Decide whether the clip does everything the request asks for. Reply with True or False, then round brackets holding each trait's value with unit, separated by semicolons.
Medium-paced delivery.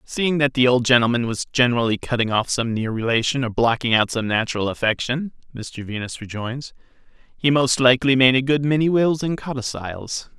True (180 wpm)